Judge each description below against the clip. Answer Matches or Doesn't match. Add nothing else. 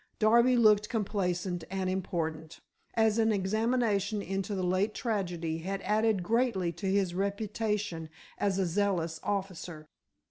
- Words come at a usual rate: Doesn't match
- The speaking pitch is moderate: Doesn't match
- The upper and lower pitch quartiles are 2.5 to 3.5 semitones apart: Matches